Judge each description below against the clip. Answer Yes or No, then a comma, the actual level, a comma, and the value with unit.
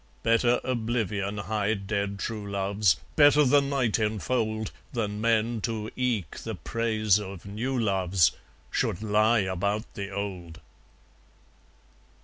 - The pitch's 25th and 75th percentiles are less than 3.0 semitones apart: Yes, narrow, 2.5 semitones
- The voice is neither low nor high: No, low, 105 Hz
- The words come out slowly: Yes, slow, 120 wpm